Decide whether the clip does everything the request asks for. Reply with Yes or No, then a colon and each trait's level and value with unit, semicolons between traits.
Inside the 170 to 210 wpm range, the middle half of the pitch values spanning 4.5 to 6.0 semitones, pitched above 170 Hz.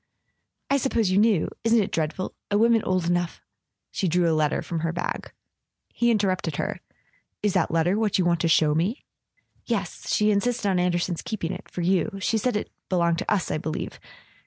No: average, 200 wpm; average, 3.8 semitones; medium, 185 Hz